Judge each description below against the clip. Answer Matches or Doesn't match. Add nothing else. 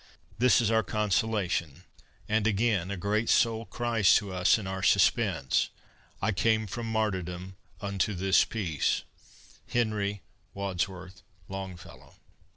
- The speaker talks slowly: Matches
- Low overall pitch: Matches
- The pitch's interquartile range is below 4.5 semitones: Matches